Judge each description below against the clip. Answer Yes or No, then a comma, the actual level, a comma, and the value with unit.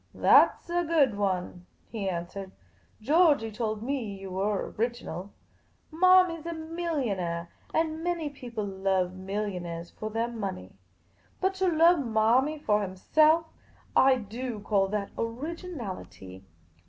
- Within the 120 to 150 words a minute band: Yes, average, 140 wpm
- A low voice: No, high, 225 Hz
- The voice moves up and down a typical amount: No, wide, 8.2 semitones